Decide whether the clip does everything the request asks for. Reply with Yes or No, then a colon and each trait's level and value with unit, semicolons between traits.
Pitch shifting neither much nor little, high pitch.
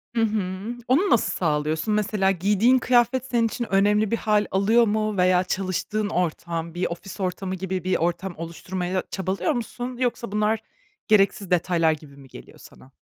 Yes: average, 3.4 semitones; high, 195 Hz